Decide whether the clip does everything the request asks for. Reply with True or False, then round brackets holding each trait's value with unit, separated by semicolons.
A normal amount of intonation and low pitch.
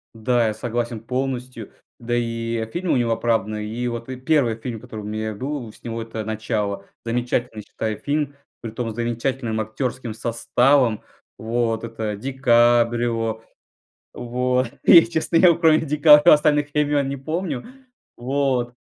True (3.1 semitones; 120 Hz)